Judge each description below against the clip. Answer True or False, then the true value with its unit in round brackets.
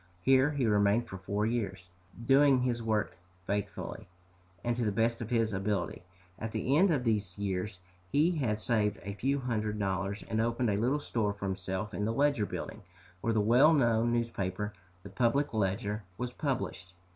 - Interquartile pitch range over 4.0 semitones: False (3.4 semitones)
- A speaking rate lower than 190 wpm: True (180 wpm)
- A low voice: True (110 Hz)